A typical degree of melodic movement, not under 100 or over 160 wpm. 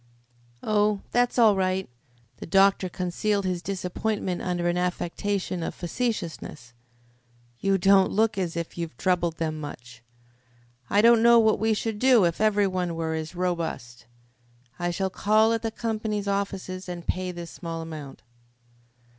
Yes: average, 3.5 semitones; average, 150 wpm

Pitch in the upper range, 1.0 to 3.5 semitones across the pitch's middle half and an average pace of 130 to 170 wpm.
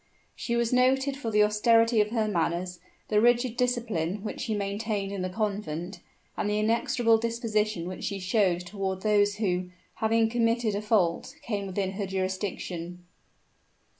Yes: high, 210 Hz; average, 3.2 semitones; average, 155 wpm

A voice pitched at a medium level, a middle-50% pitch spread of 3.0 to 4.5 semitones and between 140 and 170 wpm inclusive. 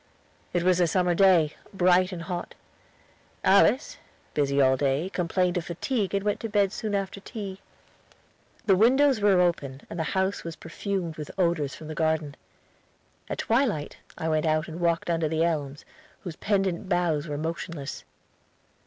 Yes: medium, 175 Hz; average, 3.5 semitones; average, 160 wpm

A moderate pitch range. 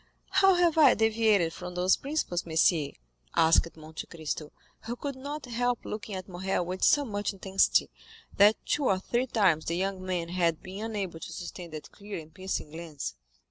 Yes: average, 5.0 semitones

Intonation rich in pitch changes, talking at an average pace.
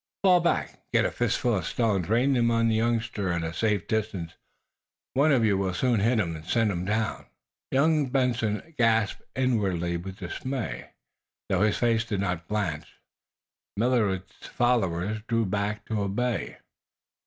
No: average, 3.9 semitones; average, 165 wpm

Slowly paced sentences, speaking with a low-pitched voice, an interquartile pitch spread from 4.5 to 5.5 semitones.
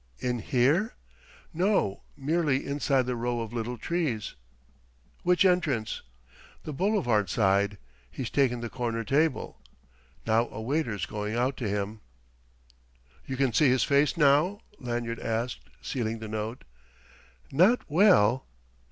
Yes: slow, 125 wpm; low, 125 Hz; average, 5.0 semitones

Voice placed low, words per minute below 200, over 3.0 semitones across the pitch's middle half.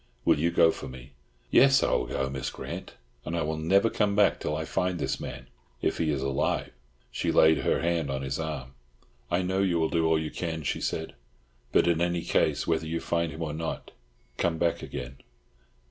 No: very low, 80 Hz; fast, 205 wpm; average, 3.8 semitones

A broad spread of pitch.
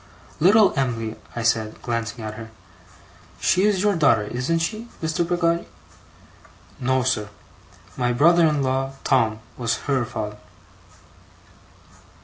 Yes: wide, 6.6 semitones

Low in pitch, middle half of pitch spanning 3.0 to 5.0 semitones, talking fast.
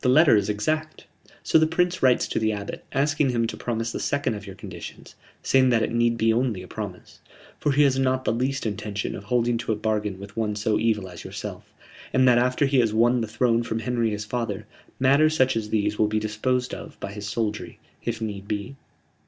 Yes: low, 115 Hz; average, 3.6 semitones; fast, 225 wpm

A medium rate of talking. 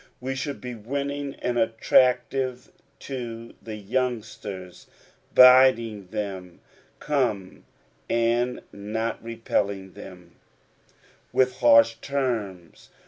No: slow, 85 wpm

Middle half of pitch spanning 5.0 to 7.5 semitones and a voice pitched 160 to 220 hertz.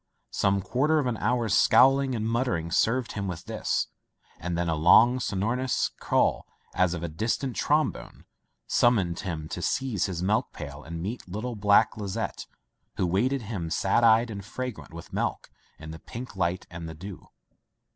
No: wide, 5.6 semitones; low, 100 Hz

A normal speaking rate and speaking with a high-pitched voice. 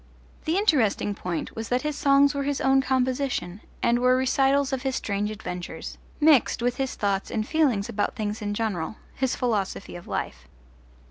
Yes: average, 175 wpm; high, 245 Hz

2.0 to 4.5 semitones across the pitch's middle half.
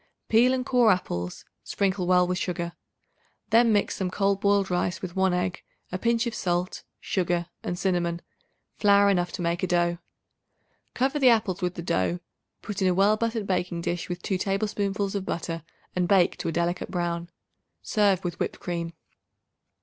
Yes: narrow, 2.5 semitones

